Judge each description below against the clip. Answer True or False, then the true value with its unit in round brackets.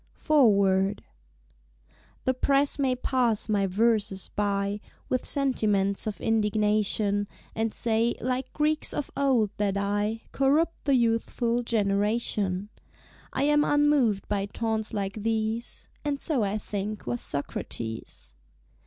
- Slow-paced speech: True (120 wpm)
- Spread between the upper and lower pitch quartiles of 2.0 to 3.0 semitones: False (4.0 semitones)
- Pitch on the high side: True (220 Hz)